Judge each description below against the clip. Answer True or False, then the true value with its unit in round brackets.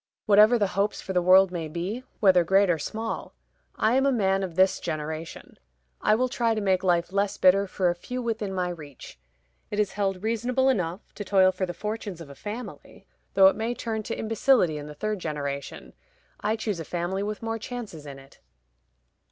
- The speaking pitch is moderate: False (195 Hz)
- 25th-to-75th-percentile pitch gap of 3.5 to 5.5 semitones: True (3.9 semitones)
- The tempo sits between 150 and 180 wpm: False (200 wpm)